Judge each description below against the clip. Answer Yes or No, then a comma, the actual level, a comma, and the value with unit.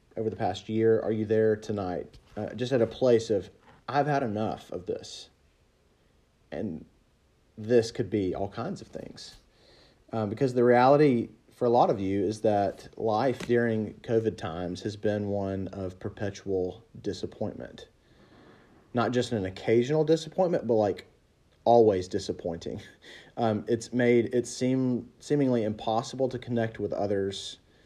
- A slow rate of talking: No, average, 145 wpm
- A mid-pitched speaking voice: No, low, 110 Hz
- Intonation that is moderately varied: Yes, average, 3.3 semitones